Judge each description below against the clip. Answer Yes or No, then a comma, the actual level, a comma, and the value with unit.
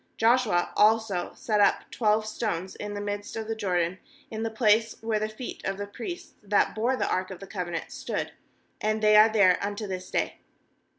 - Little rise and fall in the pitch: Yes, narrow, 2.3 semitones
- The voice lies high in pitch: Yes, high, 210 Hz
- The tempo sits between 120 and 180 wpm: No, average, 195 wpm